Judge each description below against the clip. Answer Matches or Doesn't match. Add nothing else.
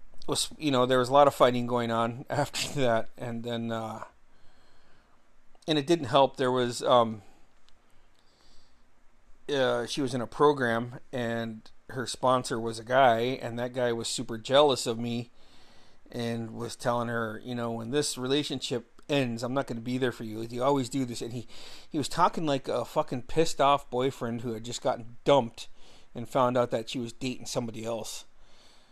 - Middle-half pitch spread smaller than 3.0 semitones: Matches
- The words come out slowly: Doesn't match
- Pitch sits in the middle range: Doesn't match